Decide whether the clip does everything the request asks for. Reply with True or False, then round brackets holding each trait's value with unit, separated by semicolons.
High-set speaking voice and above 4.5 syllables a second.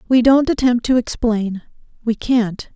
False (235 Hz; 4.2 syllables/s)